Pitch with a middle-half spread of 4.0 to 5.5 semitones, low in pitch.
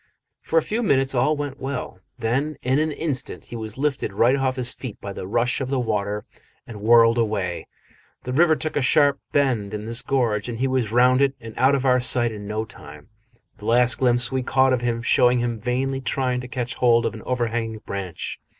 No: average, 2.9 semitones; low, 125 Hz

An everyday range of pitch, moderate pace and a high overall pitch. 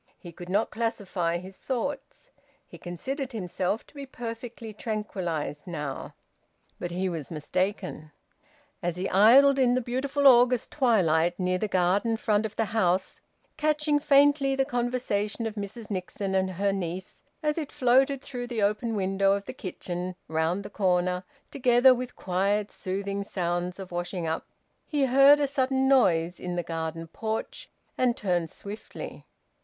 No: wide, 5.7 semitones; average, 155 wpm; high, 205 Hz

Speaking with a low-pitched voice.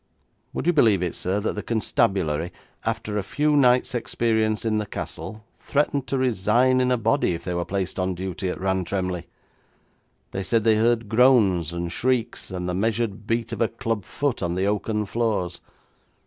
Yes: low, 105 Hz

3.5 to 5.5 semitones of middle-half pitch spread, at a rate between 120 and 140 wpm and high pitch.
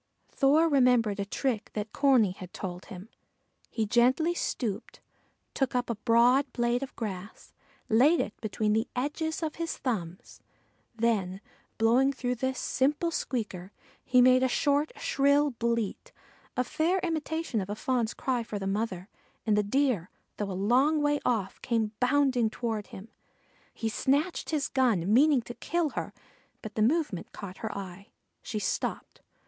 No: average, 4.8 semitones; average, 155 wpm; high, 240 Hz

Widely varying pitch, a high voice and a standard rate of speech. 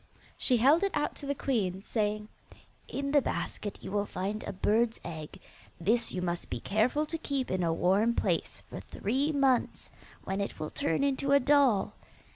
Yes: wide, 6.3 semitones; high, 225 Hz; average, 185 wpm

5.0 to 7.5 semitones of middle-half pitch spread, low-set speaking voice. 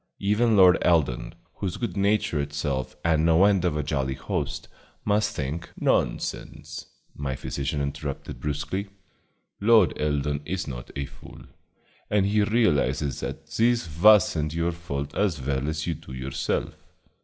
Yes: wide, 5.6 semitones; very low, 75 Hz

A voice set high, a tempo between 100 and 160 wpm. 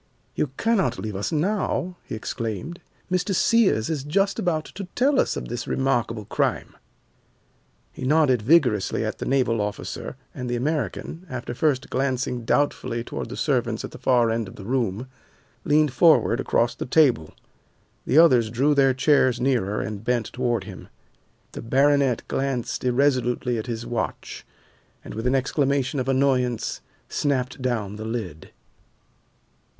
No: low, 125 Hz; average, 150 wpm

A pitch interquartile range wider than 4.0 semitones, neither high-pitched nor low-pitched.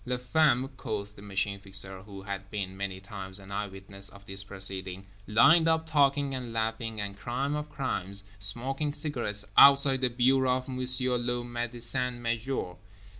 No: average, 4.6 semitones; low, 115 Hz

